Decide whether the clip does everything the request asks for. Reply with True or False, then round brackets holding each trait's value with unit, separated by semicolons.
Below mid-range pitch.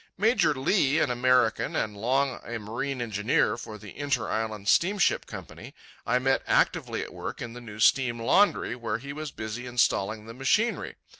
True (125 Hz)